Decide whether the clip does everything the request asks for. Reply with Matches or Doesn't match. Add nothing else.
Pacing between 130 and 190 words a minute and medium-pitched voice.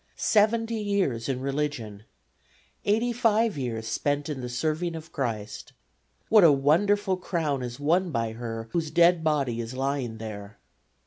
Matches